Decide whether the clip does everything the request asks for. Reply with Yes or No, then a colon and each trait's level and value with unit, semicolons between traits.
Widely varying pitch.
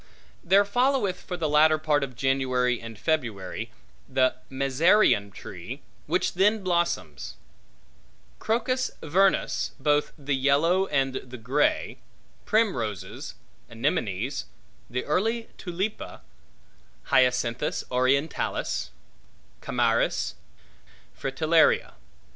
Yes: wide, 6.3 semitones